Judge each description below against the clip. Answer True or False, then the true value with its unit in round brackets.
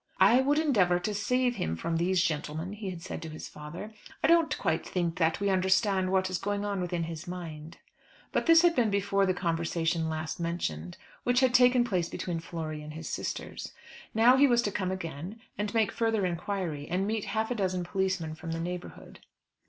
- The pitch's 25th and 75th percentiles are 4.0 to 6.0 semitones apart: True (4.3 semitones)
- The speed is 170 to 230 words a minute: True (200 wpm)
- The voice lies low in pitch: False (185 Hz)